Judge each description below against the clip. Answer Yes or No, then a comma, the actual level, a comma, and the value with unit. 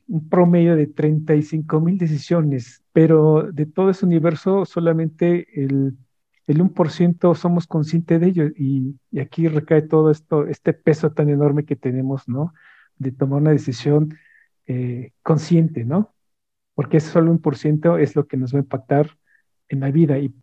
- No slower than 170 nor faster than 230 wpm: No, average, 160 wpm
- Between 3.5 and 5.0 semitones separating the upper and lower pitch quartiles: No, average, 3.1 semitones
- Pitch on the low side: No, medium, 155 Hz